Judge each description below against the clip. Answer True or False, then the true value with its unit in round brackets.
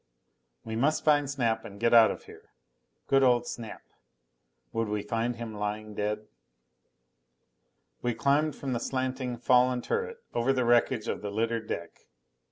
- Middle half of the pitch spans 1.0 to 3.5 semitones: True (2.9 semitones)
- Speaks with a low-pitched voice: True (120 Hz)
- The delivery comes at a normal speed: True (155 wpm)